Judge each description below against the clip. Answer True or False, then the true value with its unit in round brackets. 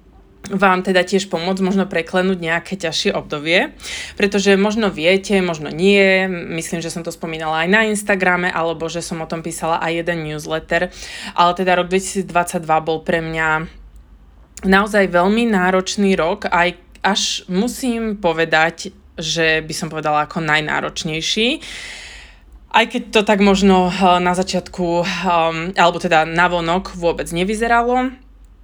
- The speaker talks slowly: False (135 wpm)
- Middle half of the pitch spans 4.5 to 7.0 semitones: False (2.9 semitones)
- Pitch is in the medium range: True (180 Hz)